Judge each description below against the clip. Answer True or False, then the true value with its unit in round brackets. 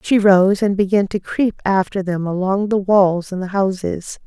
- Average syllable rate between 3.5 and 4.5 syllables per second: True (4.4 syllables/s)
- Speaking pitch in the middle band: False (195 Hz)